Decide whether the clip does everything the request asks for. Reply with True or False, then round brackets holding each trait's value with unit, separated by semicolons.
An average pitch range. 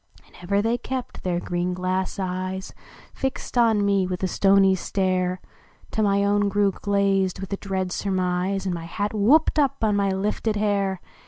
False (1.8 semitones)